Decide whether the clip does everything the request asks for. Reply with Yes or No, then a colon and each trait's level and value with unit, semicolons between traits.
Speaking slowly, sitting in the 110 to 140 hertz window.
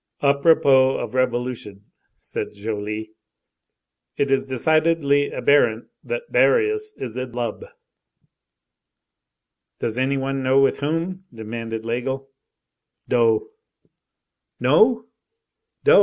Yes: slow, 95 wpm; low, 135 Hz